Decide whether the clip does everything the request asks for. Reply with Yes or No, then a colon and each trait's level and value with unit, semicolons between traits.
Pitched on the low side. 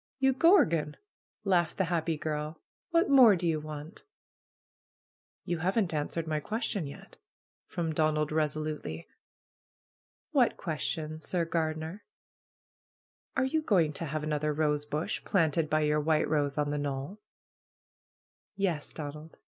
No: medium, 155 Hz